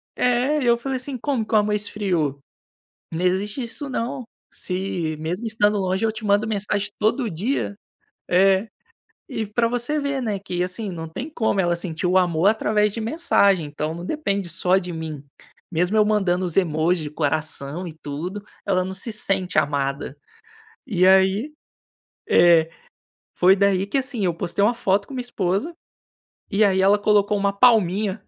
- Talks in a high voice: Yes, high, 195 Hz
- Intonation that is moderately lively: Yes, average, 3.8 semitones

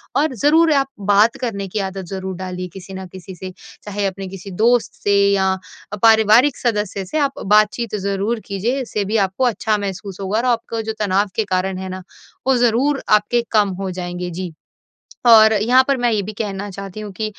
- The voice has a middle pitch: No, high, 205 Hz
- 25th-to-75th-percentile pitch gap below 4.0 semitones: Yes, average, 3.2 semitones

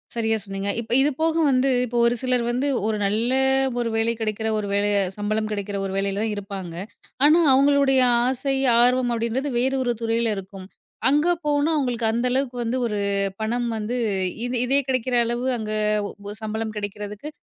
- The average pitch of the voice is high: Yes, high, 235 Hz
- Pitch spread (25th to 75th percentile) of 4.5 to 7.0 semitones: No, average, 3.4 semitones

